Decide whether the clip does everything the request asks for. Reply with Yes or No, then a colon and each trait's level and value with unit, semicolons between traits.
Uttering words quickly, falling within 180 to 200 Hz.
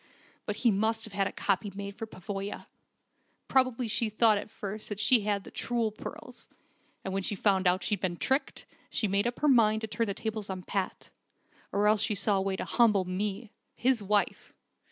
No: fast, 210 wpm; high, 210 Hz